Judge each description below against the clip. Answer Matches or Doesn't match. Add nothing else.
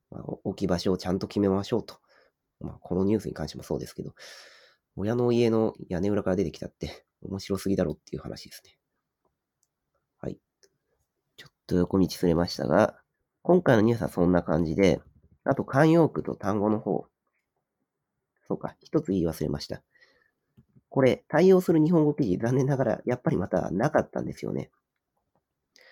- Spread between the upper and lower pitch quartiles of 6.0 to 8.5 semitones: Matches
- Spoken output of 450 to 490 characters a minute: Doesn't match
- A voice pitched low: Matches